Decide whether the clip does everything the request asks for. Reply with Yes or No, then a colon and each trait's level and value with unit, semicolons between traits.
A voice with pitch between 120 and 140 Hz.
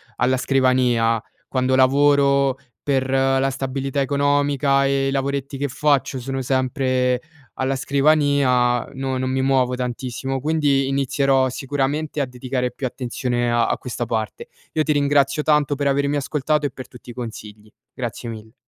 Yes: low, 135 Hz